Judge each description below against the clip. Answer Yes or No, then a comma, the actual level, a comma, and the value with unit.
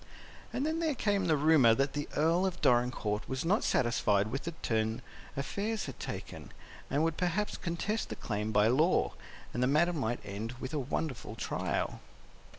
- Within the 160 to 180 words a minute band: Yes, average, 175 wpm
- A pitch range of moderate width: No, wide, 6.8 semitones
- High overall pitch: No, medium, 140 Hz